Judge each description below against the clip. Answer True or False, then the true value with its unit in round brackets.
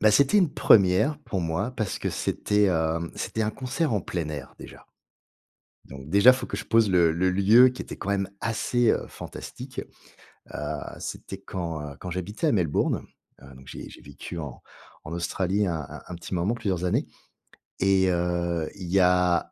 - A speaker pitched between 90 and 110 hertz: True (95 Hz)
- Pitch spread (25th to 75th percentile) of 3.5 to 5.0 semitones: True (4.1 semitones)